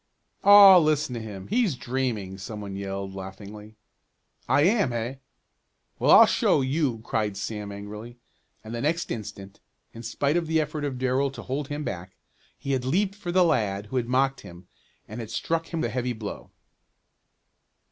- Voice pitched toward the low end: Yes, low, 125 Hz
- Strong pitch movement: Yes, wide, 6.2 semitones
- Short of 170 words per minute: No, average, 175 wpm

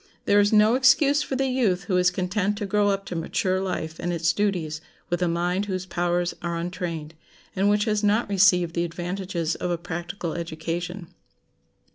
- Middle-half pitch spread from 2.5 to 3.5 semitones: Yes, average, 3.0 semitones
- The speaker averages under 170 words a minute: No, average, 185 wpm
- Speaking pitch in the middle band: Yes, medium, 180 Hz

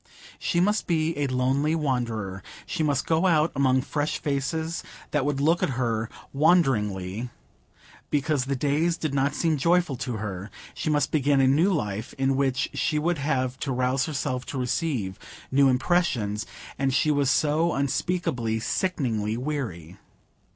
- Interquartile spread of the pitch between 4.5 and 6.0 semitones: No, average, 3.8 semitones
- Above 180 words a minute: No, average, 155 wpm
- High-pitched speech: No, medium, 140 Hz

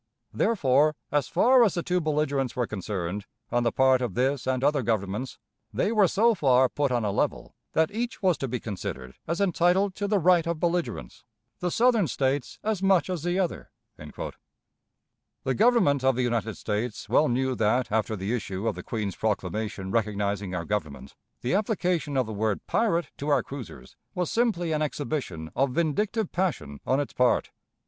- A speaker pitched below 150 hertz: Yes, low, 135 Hz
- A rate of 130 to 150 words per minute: No, average, 180 wpm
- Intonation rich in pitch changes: Yes, wide, 8.2 semitones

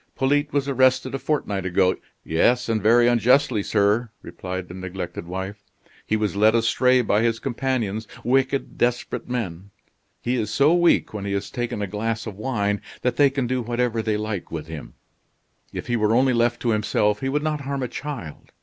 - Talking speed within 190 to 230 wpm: Yes, average, 195 wpm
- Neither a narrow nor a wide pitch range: Yes, average, 4.1 semitones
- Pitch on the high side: No, low, 115 Hz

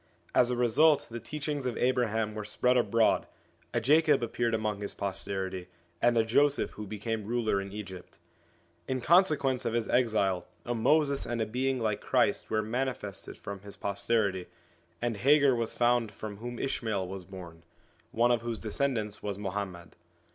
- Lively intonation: No, average, 3.5 semitones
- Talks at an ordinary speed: Yes, average, 170 wpm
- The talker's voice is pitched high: No, low, 115 Hz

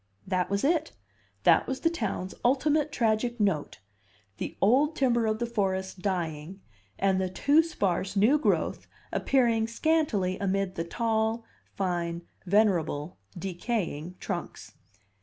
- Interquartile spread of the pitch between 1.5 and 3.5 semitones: No, average, 4.6 semitones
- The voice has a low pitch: No, high, 205 Hz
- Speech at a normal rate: No, slow, 125 wpm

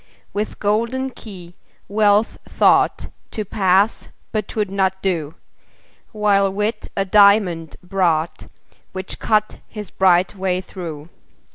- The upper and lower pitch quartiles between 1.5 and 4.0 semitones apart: Yes, narrow, 2.6 semitones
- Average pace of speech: No, slow, 115 wpm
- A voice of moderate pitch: No, high, 195 Hz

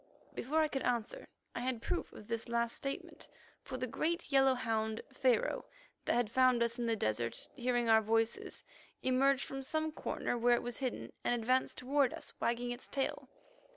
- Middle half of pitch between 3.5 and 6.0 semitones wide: No, narrow, 2.5 semitones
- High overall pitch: Yes, high, 245 Hz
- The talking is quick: No, average, 185 wpm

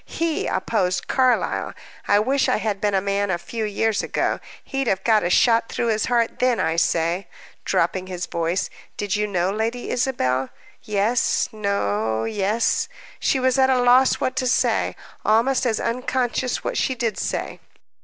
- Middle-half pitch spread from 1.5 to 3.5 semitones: No, average, 4.7 semitones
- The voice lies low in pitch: No, high, 220 Hz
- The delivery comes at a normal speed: Yes, average, 170 wpm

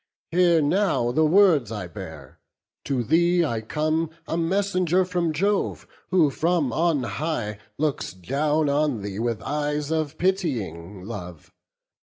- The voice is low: No, medium, 150 Hz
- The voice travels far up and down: Yes, wide, 6.7 semitones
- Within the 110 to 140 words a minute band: Yes, slow, 135 wpm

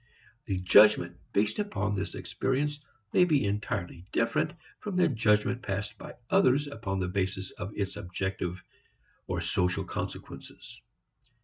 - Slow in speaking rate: Yes, slow, 130 wpm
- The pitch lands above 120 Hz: No, low, 105 Hz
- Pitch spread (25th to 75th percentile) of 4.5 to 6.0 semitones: Yes, wide, 5.5 semitones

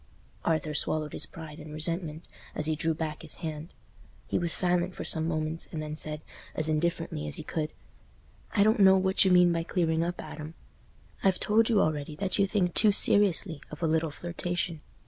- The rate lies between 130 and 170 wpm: No, average, 195 wpm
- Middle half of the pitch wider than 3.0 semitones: No, narrow, 2.5 semitones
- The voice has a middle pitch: Yes, medium, 165 Hz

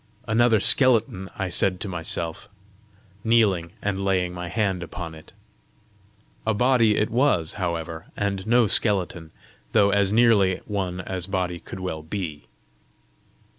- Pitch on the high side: No, very low, 95 Hz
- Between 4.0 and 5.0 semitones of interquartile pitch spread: No, average, 3.4 semitones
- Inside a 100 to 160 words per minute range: Yes, slow, 135 wpm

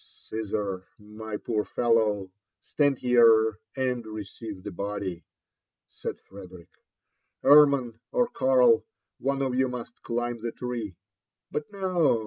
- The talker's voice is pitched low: Yes, low, 115 Hz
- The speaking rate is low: Yes, slow, 125 wpm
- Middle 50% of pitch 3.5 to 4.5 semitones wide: Yes, average, 3.8 semitones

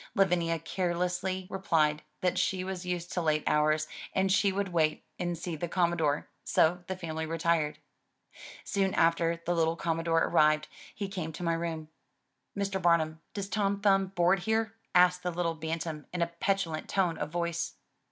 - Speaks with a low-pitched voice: No, medium, 170 Hz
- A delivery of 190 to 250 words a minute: No, average, 165 wpm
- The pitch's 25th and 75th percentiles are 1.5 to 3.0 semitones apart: Yes, narrow, 2.5 semitones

